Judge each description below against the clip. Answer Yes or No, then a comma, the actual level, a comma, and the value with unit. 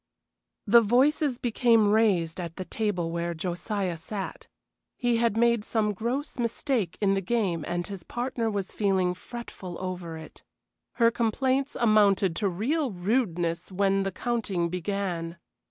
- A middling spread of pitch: Yes, average, 4.7 semitones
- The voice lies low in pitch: No, high, 200 Hz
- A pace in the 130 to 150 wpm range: Yes, average, 140 wpm